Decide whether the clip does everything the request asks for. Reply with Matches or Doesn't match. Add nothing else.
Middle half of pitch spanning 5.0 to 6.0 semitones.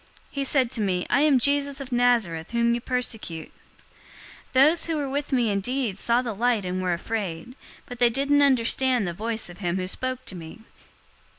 Matches